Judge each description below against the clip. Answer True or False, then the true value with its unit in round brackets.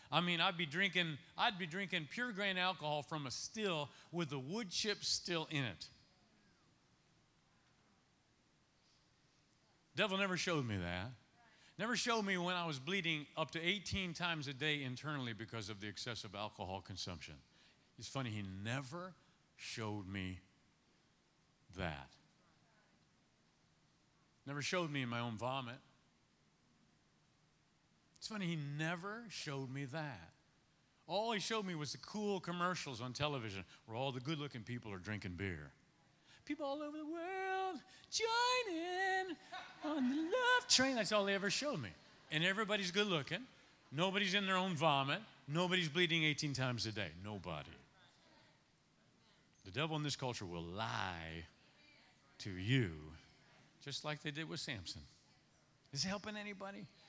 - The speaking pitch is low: False (155 Hz)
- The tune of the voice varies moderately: False (8.3 semitones)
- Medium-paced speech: True (145 wpm)